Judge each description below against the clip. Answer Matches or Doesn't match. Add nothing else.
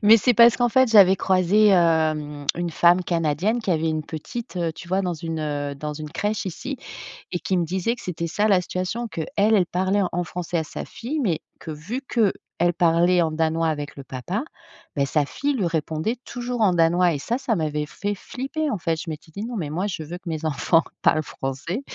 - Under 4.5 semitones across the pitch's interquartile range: Doesn't match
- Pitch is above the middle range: Doesn't match